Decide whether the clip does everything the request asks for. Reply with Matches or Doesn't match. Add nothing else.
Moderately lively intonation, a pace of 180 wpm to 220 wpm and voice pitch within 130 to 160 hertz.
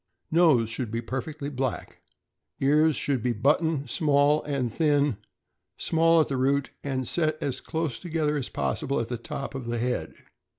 Doesn't match